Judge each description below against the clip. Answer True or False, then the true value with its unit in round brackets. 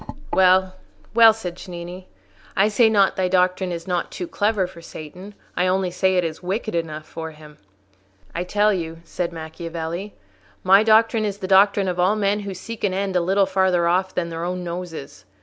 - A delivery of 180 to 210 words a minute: True (190 wpm)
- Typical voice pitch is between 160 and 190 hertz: True (185 Hz)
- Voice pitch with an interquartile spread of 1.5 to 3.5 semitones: True (2.6 semitones)